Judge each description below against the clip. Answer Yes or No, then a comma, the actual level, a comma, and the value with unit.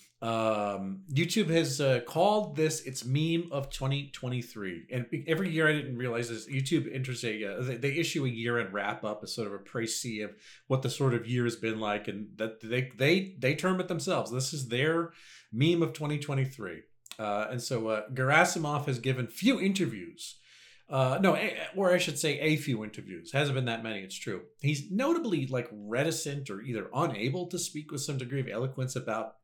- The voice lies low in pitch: Yes, low, 130 Hz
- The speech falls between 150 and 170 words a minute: No, average, 190 wpm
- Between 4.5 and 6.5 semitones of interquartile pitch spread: Yes, average, 5.3 semitones